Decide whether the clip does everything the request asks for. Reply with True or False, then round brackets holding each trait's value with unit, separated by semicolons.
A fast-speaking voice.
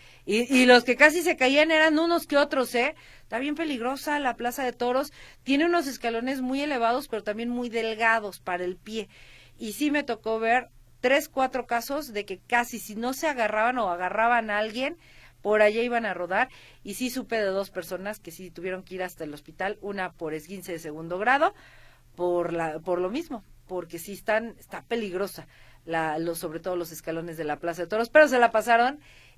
True (205 wpm)